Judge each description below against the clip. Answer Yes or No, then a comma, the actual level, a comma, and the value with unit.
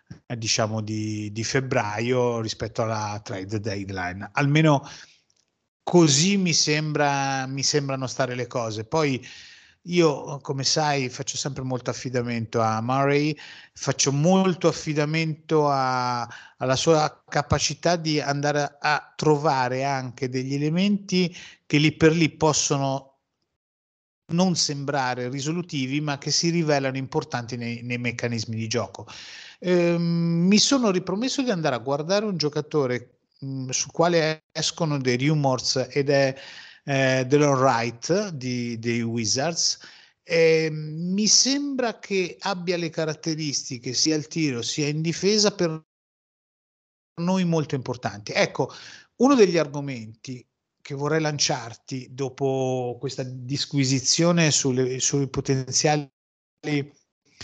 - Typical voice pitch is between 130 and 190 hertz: Yes, medium, 140 Hz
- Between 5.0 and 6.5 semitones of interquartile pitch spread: No, average, 4.0 semitones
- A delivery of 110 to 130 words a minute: Yes, slow, 115 wpm